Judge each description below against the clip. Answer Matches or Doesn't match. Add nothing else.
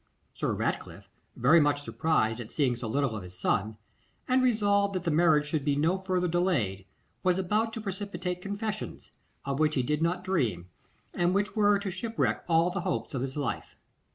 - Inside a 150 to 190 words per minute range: Matches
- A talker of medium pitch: Matches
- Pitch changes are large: Matches